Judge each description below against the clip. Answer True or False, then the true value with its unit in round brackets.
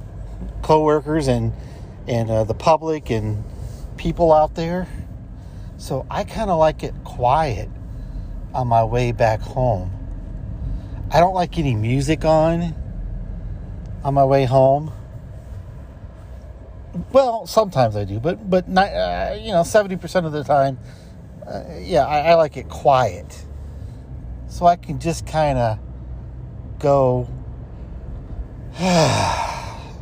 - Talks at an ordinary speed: False (120 wpm)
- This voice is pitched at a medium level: False (125 Hz)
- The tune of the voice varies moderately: False (7.3 semitones)